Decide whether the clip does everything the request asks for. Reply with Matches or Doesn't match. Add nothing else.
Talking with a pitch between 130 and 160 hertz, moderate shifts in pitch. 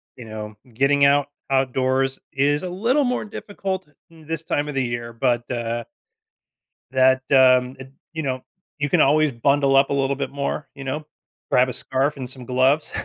Doesn't match